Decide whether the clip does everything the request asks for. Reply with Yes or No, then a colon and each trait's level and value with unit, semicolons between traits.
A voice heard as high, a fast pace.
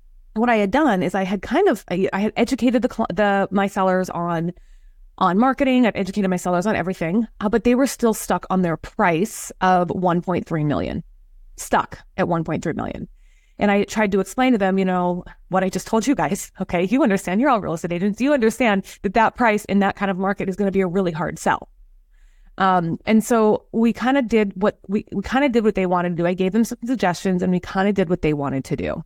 Yes: high, 195 Hz; fast, 235 wpm